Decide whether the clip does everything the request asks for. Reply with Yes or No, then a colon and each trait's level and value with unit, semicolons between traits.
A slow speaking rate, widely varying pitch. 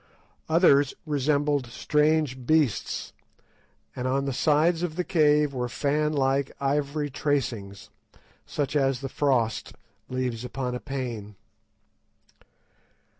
No: slow, 105 wpm; average, 2.7 semitones